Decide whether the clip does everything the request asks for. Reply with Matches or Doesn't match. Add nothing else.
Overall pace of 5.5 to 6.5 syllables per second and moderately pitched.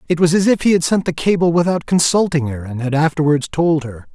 Matches